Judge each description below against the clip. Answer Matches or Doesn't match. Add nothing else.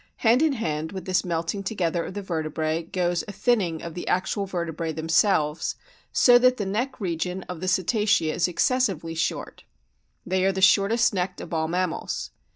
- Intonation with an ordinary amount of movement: Matches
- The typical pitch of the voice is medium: Matches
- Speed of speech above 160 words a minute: Matches